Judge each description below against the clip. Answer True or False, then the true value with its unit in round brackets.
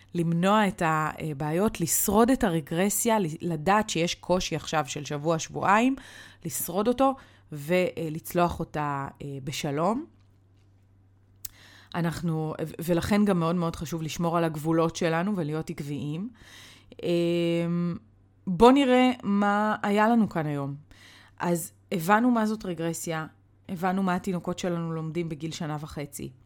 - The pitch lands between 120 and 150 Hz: False (165 Hz)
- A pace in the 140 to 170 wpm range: False (115 wpm)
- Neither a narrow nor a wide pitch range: True (3.8 semitones)